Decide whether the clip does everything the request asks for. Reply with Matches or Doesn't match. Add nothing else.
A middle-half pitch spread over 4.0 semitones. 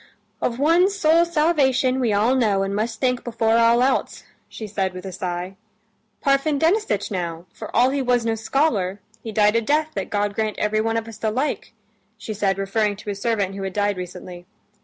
Matches